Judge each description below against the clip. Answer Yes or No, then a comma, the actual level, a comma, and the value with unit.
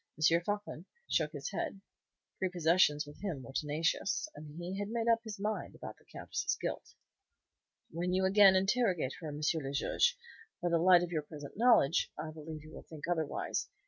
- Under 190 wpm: Yes, average, 175 wpm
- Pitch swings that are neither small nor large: Yes, average, 4.2 semitones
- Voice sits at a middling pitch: Yes, medium, 170 Hz